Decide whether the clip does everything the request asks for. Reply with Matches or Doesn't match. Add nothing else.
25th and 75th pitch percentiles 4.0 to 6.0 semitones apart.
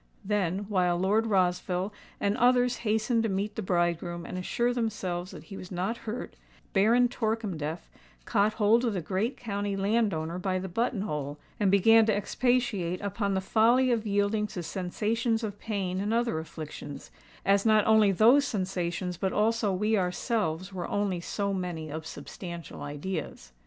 Doesn't match